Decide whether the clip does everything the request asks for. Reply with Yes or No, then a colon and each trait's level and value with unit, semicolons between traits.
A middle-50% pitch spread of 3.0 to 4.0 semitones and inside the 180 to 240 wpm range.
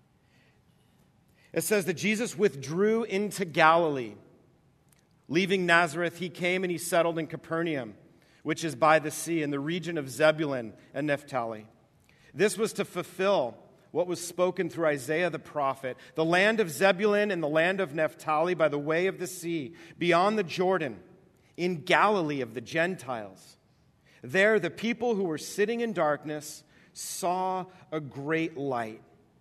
No: average, 3.4 semitones; average, 150 wpm